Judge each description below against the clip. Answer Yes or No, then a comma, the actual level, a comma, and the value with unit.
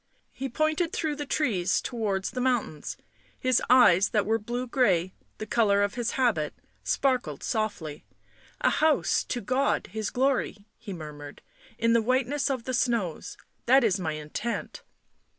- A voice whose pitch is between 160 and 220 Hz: No, high, 235 Hz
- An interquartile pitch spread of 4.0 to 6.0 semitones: Yes, average, 4.6 semitones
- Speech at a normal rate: Yes, average, 160 wpm